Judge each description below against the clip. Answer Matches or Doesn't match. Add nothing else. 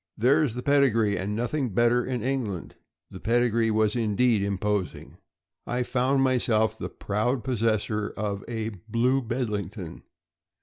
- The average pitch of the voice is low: Matches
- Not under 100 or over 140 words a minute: Matches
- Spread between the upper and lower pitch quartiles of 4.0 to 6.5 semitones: Doesn't match